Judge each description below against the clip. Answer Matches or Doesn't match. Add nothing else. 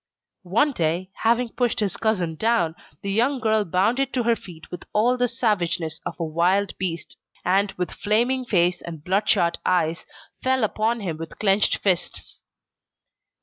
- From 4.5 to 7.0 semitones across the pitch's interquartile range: Matches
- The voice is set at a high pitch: Matches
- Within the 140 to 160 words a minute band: Matches